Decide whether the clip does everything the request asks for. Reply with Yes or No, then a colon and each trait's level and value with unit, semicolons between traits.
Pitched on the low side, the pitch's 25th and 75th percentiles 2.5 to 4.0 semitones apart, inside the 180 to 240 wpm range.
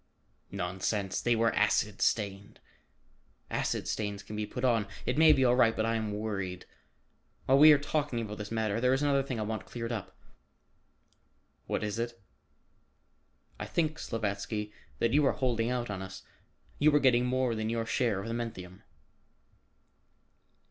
No: low, 115 Hz; average, 3.3 semitones; average, 170 wpm